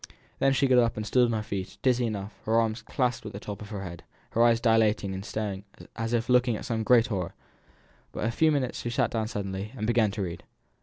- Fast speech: Yes, fast, 250 wpm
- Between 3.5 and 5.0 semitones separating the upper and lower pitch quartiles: No, average, 2.7 semitones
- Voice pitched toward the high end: No, low, 110 Hz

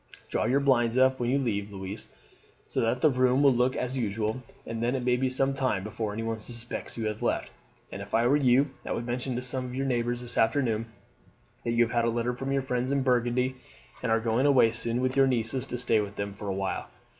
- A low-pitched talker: Yes, low, 120 Hz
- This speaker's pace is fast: Yes, fast, 250 wpm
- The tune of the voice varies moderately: No, narrow, 2.3 semitones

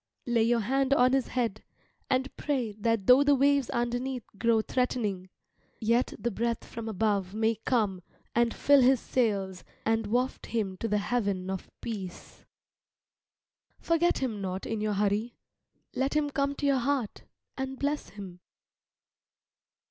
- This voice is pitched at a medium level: No, high, 235 Hz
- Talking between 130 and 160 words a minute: Yes, average, 150 wpm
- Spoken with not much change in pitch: No, average, 4.1 semitones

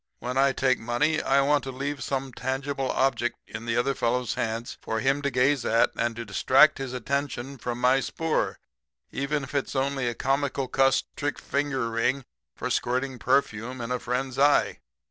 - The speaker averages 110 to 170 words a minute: No, average, 185 wpm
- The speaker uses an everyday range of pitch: No, narrow, 2.3 semitones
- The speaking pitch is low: Yes, low, 130 Hz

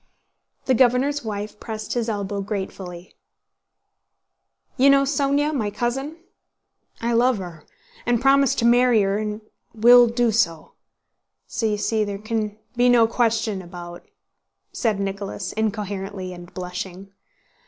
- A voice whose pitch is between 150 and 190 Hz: No, high, 220 Hz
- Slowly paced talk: Yes, slow, 130 wpm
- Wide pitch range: No, average, 3.6 semitones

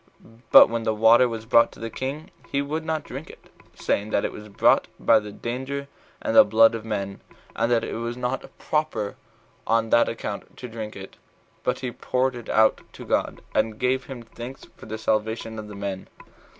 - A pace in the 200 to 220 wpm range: Yes, fast, 205 wpm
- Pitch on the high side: No, low, 115 Hz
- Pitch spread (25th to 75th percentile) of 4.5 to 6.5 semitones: No, average, 2.7 semitones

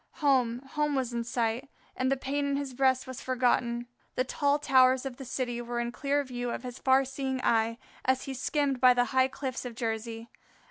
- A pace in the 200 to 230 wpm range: Yes, fast, 205 wpm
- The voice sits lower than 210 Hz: No, very high, 255 Hz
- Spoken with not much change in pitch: Yes, narrow, 2.1 semitones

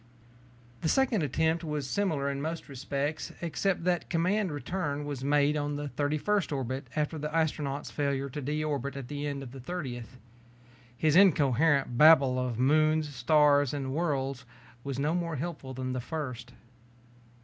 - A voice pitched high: No, medium, 145 Hz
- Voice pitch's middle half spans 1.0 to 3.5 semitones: Yes, average, 2.8 semitones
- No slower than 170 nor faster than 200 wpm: No, average, 160 wpm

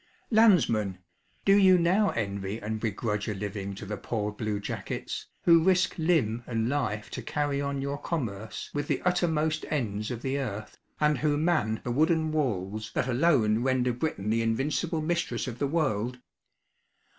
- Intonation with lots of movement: Yes, wide, 6.5 semitones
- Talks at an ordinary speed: Yes, average, 165 wpm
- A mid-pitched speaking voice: No, low, 125 Hz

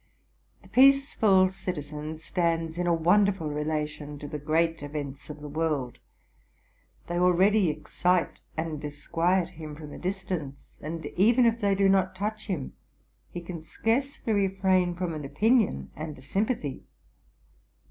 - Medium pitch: Yes, medium, 170 Hz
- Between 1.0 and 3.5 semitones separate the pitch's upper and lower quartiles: No, average, 4.2 semitones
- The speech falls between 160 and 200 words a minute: No, average, 140 wpm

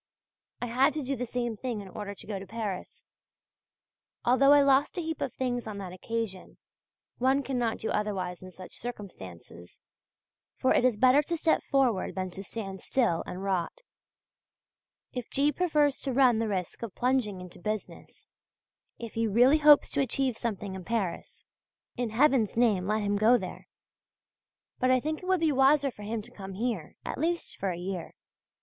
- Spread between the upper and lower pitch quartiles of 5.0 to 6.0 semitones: Yes, wide, 5.4 semitones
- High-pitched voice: Yes, high, 230 Hz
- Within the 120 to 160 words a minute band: No, average, 180 wpm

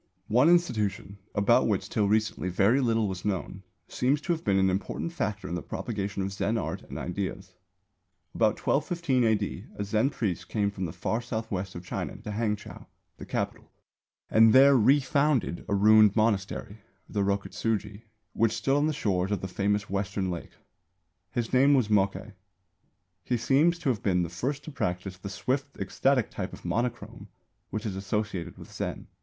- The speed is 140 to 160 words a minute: No, average, 175 wpm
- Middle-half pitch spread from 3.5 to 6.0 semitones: Yes, average, 4.3 semitones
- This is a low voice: Yes, low, 105 Hz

